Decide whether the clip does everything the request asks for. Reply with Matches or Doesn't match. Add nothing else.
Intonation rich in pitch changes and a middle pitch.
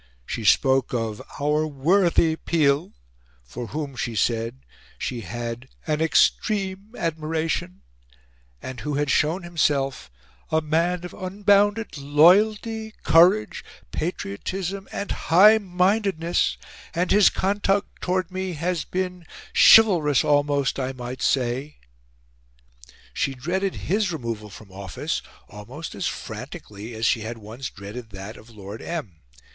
Matches